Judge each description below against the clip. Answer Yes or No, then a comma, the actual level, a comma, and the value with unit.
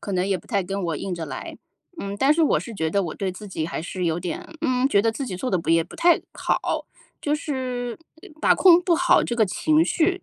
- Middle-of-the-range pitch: No, high, 205 Hz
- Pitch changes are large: Yes, wide, 7.8 semitones